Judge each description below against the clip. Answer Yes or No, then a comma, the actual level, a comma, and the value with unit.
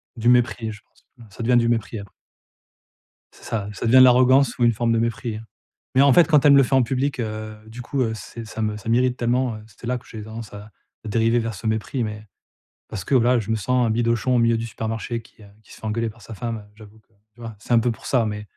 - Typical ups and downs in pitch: No, narrow, 2.1 semitones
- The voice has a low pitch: Yes, low, 115 Hz